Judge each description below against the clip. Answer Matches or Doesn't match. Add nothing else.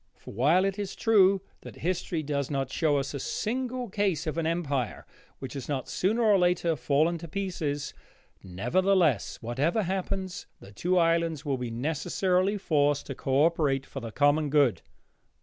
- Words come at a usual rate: Matches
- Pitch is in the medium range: Matches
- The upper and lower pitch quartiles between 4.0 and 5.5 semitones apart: Matches